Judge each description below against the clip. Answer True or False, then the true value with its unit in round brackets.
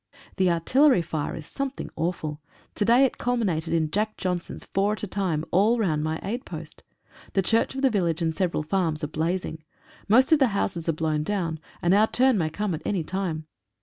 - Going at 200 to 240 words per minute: True (205 wpm)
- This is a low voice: False (185 Hz)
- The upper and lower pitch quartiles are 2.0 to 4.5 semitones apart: False (5.0 semitones)